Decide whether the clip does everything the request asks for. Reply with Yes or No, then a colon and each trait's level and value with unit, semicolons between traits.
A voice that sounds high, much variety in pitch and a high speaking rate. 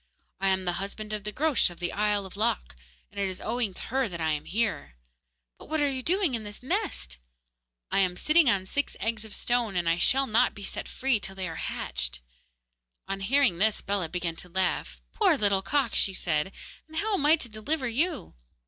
Yes: high, 210 Hz; wide, 5.8 semitones; fast, 220 wpm